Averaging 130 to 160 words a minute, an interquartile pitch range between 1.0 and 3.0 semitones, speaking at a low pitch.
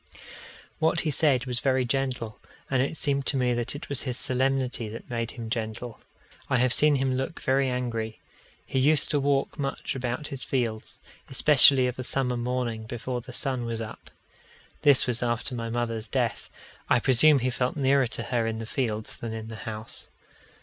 No: average, 185 wpm; average, 2.7 semitones; low, 125 Hz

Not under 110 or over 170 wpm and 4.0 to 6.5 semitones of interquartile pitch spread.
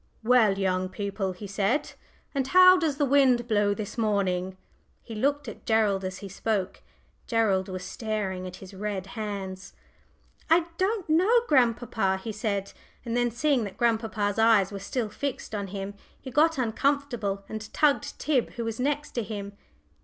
Yes: average, 160 wpm; average, 4.7 semitones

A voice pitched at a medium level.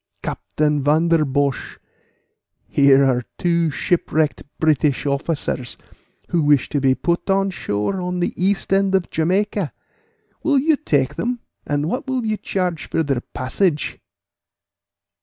Yes: medium, 160 Hz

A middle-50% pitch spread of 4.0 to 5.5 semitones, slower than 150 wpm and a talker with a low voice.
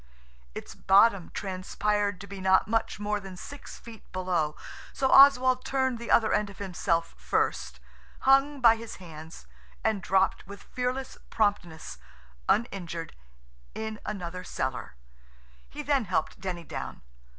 No: average, 4.4 semitones; slow, 135 wpm; high, 200 Hz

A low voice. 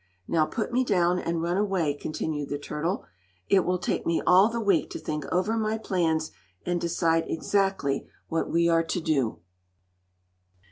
No: medium, 170 Hz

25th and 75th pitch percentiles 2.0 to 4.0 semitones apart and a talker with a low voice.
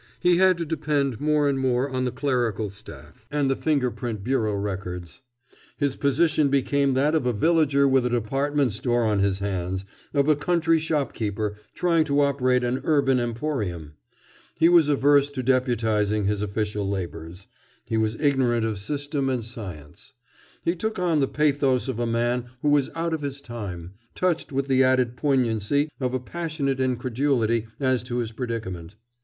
No: average, 4.6 semitones; low, 130 Hz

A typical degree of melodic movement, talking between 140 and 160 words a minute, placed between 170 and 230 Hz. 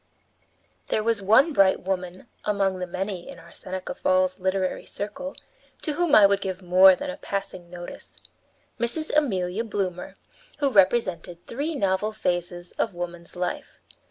Yes: average, 3.3 semitones; average, 150 wpm; high, 190 Hz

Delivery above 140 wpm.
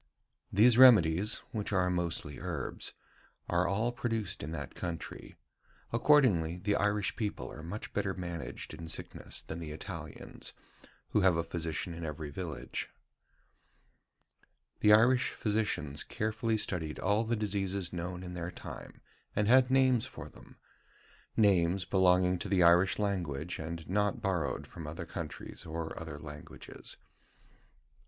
No: slow, 135 wpm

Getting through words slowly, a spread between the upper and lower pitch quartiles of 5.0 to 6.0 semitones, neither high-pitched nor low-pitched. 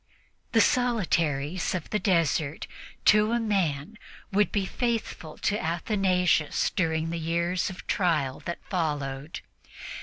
No: slow, 120 wpm; average, 4.6 semitones; medium, 175 Hz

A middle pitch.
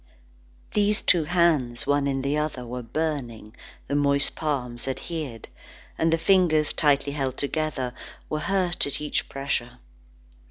Yes: medium, 145 Hz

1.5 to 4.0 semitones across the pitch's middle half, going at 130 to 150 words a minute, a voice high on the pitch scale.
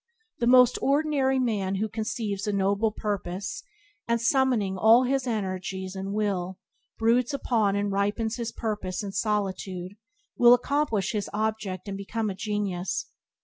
Yes: average, 3.3 semitones; average, 145 wpm; high, 210 Hz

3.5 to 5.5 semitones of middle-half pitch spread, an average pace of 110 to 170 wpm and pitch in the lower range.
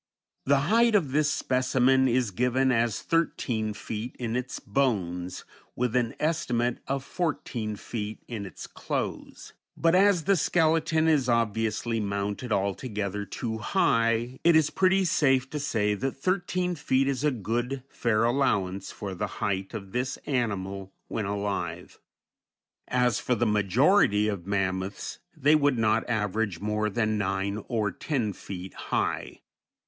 Yes: average, 5.0 semitones; average, 145 wpm; low, 120 Hz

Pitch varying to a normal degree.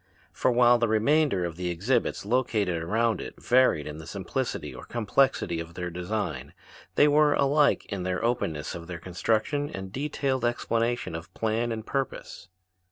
No: wide, 6.2 semitones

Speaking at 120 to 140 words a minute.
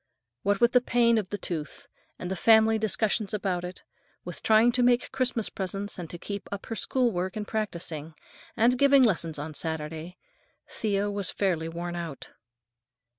No: average, 170 wpm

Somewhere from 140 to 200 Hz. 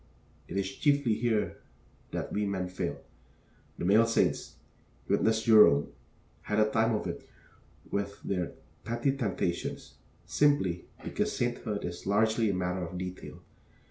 No: low, 105 Hz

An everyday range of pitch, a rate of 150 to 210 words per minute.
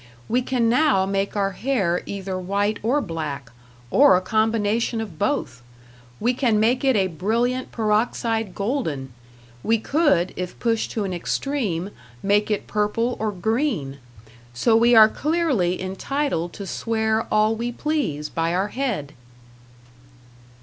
No: average, 4.5 semitones; average, 140 wpm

